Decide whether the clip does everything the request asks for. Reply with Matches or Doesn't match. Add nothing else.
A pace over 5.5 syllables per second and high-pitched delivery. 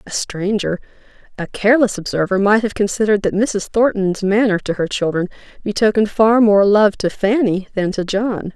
Doesn't match